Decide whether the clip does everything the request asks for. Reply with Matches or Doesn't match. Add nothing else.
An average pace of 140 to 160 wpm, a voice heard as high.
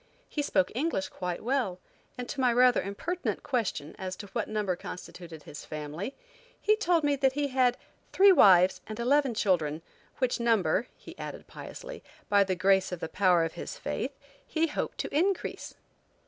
Doesn't match